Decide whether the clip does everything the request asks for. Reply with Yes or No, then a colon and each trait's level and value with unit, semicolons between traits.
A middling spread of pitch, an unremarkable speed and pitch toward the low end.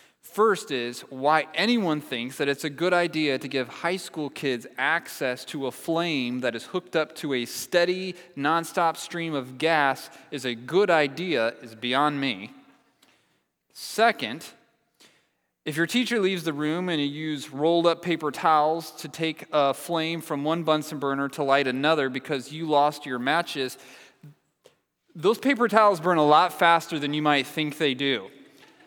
No: average, 3.5 semitones; average, 165 wpm; medium, 155 Hz